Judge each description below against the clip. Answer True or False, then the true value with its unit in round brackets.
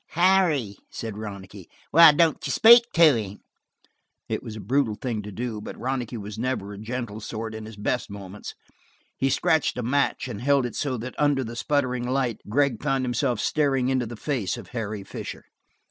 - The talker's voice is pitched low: True (120 Hz)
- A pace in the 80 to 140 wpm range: False (190 wpm)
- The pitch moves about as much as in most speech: True (4.4 semitones)